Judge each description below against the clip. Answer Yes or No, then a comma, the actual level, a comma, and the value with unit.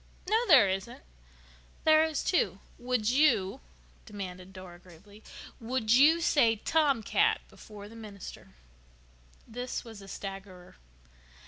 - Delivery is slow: Yes, slow, 115 wpm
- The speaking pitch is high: Yes, high, 220 Hz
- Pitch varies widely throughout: Yes, wide, 6.0 semitones